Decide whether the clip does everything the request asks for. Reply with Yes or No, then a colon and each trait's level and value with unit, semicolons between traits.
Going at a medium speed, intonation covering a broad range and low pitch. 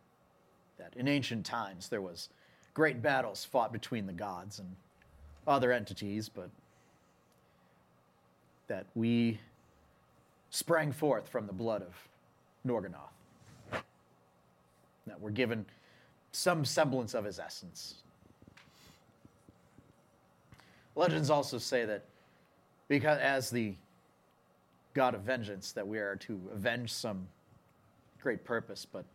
No: slow, 105 wpm; wide, 5.8 semitones; low, 110 Hz